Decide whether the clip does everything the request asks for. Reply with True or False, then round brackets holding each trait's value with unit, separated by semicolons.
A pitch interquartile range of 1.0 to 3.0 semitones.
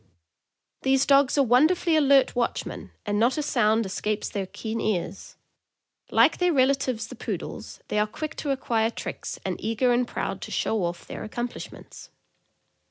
False (4.3 semitones)